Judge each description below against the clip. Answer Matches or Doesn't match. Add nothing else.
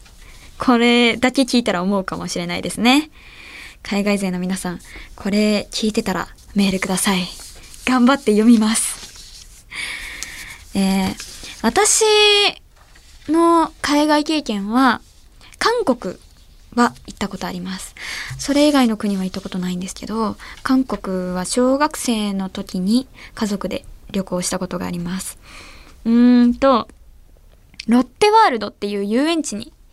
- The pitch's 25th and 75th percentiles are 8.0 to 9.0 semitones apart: Doesn't match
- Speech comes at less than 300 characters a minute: Matches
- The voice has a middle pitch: Doesn't match